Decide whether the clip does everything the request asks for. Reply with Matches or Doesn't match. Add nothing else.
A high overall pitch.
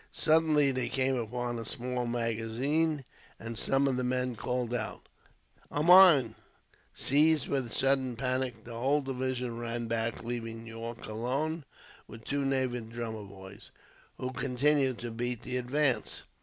Doesn't match